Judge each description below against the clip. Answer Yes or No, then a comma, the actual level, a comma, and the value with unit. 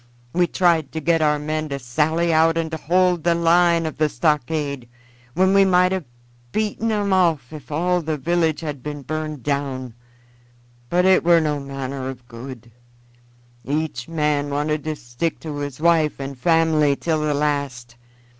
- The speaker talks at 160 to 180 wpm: Yes, average, 165 wpm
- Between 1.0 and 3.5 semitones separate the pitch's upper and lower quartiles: Yes, average, 3.1 semitones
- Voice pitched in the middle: Yes, medium, 155 Hz